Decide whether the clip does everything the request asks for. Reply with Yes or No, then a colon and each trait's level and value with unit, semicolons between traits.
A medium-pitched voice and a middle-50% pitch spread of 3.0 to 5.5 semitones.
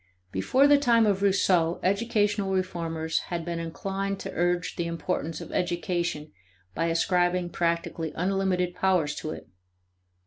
No: medium, 175 Hz; narrow, 2.6 semitones